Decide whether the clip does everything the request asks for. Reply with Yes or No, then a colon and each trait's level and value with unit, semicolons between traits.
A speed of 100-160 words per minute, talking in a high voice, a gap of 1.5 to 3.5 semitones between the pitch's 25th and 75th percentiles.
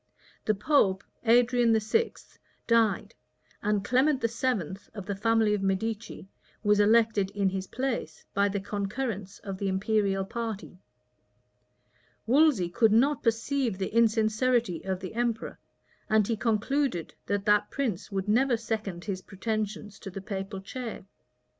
Yes: slow, 135 wpm; high, 215 Hz; average, 3.0 semitones